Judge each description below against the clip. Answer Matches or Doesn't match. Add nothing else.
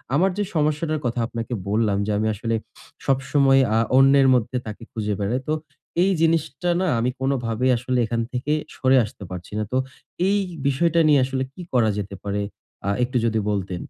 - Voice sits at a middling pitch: Doesn't match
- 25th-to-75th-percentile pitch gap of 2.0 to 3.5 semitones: Doesn't match